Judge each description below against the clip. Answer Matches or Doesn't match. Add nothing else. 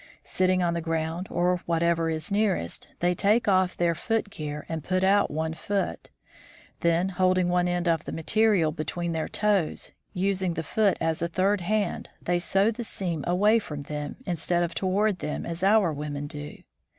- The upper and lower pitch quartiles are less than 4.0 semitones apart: Matches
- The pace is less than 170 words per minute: Doesn't match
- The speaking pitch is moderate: Matches